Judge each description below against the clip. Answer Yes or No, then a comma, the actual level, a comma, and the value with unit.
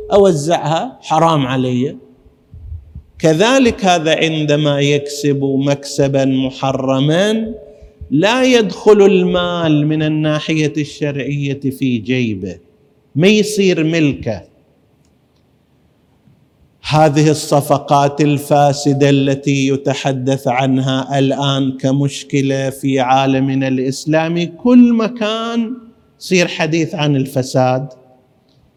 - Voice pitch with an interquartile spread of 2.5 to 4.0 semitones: Yes, average, 3.4 semitones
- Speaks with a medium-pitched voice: Yes, medium, 145 Hz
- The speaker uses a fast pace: No, average, 75 wpm